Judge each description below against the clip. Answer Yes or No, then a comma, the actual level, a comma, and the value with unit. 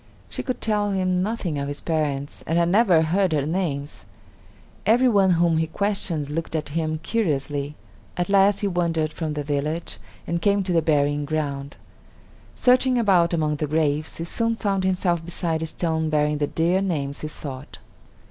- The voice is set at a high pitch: No, medium, 165 Hz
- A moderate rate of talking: Yes, average, 175 wpm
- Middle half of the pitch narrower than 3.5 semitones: No, average, 4.1 semitones